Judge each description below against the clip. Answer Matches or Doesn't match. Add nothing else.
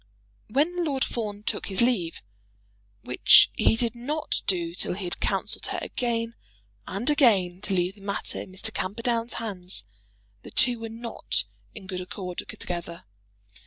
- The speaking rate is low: Doesn't match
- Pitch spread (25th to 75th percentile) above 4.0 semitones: Matches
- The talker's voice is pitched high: Matches